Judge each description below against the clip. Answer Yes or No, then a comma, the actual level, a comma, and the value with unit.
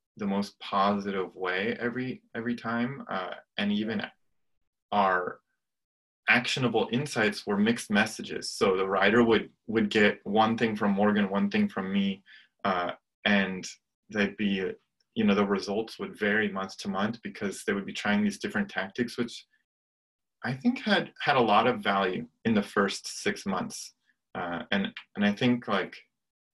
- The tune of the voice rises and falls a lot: No, average, 3.2 semitones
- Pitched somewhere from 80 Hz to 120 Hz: Yes, low, 105 Hz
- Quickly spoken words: No, average, 160 wpm